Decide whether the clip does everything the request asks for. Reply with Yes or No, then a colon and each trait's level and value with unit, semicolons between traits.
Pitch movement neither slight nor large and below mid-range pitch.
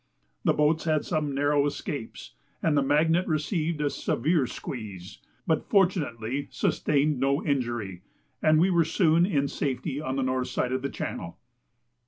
No: average, 3.3 semitones; medium, 145 Hz